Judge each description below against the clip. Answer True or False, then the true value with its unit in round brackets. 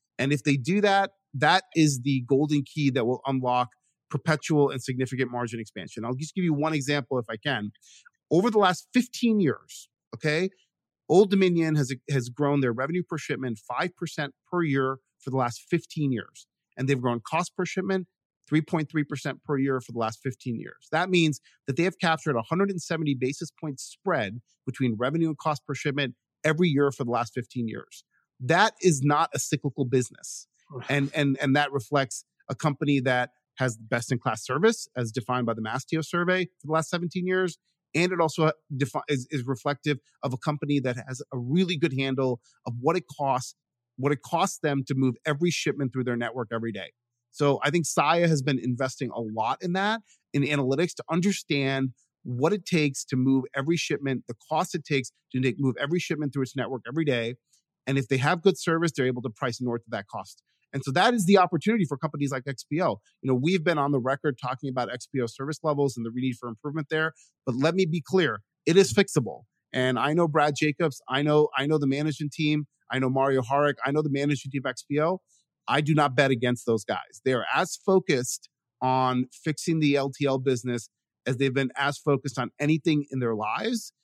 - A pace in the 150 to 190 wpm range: False (200 wpm)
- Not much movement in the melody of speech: False (3.7 semitones)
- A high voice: False (140 Hz)